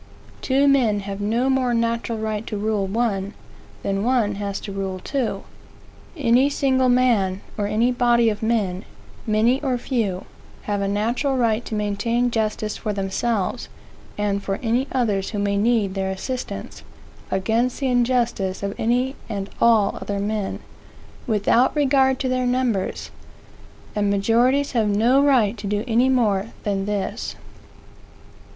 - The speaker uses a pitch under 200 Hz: No, high, 225 Hz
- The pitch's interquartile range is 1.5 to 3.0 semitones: No, average, 3.6 semitones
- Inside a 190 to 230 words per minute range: No, average, 145 wpm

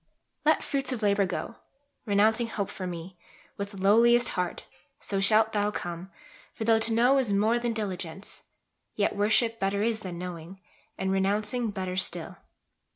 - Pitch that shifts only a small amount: No, average, 3.0 semitones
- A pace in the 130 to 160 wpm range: Yes, average, 155 wpm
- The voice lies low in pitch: No, high, 205 Hz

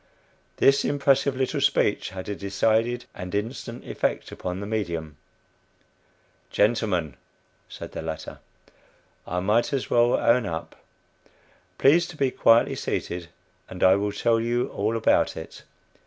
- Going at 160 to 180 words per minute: No, slow, 135 wpm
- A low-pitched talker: Yes, low, 110 Hz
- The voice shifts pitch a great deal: No, average, 4.7 semitones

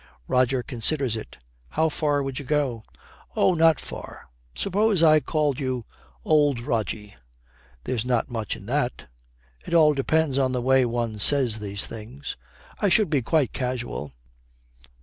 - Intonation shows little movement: No, average, 4.3 semitones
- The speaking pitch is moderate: No, low, 130 Hz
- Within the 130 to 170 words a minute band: Yes, average, 150 wpm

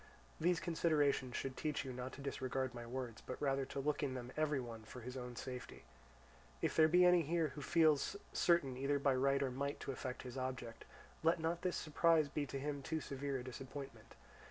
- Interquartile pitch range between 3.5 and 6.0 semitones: No, average, 3.1 semitones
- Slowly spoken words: No, fast, 205 wpm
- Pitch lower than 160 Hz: Yes, medium, 140 Hz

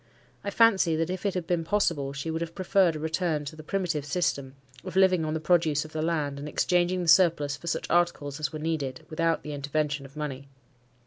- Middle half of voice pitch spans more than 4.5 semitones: No, average, 3.1 semitones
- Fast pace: Yes, fast, 220 wpm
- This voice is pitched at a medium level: Yes, medium, 160 Hz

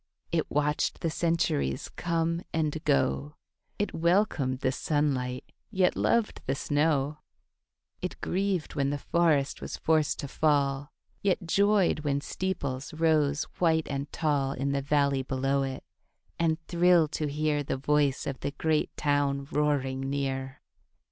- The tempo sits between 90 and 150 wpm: Yes, average, 140 wpm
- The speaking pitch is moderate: Yes, medium, 145 Hz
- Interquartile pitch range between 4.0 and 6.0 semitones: No, average, 2.9 semitones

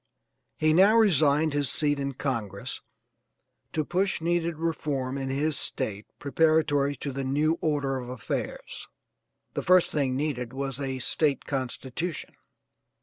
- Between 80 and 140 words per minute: Yes, slow, 135 wpm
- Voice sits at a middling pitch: Yes, medium, 145 Hz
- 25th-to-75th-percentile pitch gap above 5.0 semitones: No, average, 3.0 semitones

